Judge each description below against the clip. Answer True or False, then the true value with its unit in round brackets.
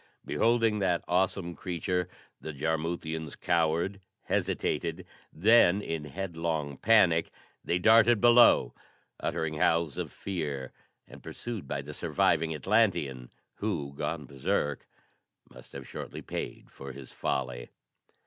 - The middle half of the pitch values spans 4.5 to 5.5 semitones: True (4.9 semitones)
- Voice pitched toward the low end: True (85 Hz)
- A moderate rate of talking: False (115 wpm)